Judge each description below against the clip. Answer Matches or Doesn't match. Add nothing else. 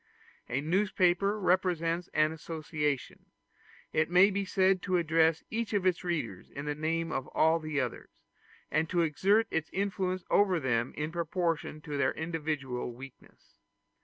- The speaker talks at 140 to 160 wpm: Matches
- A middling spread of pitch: Matches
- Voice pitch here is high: Doesn't match